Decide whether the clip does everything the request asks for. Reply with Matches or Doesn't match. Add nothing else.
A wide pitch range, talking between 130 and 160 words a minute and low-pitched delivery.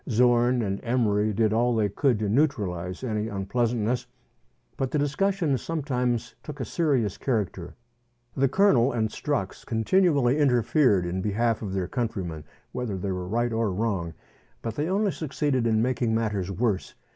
Doesn't match